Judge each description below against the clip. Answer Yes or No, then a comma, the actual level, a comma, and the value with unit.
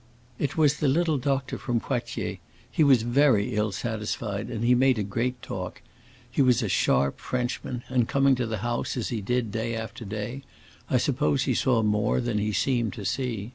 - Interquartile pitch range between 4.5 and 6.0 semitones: No, average, 3.3 semitones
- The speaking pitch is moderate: No, low, 120 Hz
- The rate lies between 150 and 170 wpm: No, average, 195 wpm